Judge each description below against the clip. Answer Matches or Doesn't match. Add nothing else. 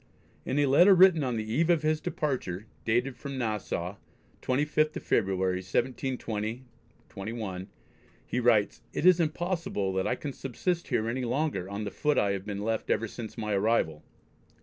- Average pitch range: Doesn't match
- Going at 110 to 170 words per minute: Matches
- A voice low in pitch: Matches